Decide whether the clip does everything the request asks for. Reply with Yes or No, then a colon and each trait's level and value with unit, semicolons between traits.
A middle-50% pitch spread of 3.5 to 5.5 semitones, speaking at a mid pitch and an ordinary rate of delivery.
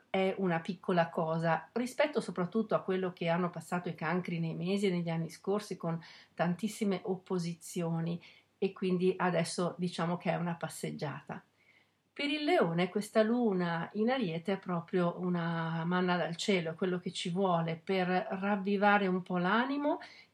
No: average, 3.1 semitones; medium, 180 Hz; average, 155 wpm